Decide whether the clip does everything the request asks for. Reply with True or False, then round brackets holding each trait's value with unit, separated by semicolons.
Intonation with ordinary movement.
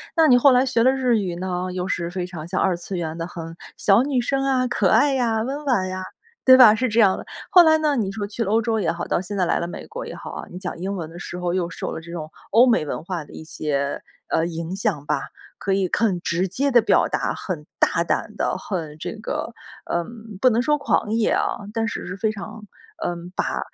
False (5.7 semitones)